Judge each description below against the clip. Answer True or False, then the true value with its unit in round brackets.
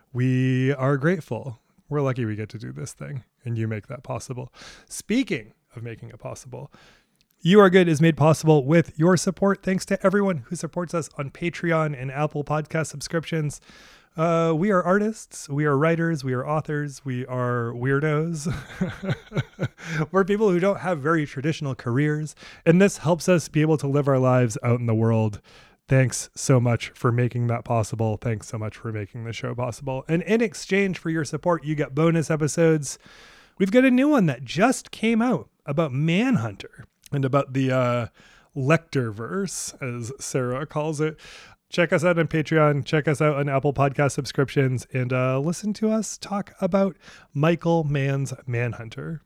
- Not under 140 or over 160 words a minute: False (175 wpm)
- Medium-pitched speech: True (150 Hz)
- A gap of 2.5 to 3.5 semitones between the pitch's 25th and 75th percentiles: False (4.7 semitones)